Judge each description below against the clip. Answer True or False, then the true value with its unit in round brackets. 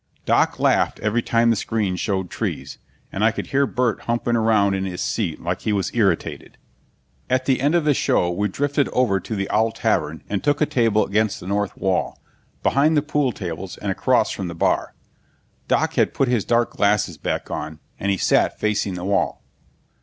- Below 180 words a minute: False (200 wpm)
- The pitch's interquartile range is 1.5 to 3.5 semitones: False (4.3 semitones)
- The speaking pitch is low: True (105 Hz)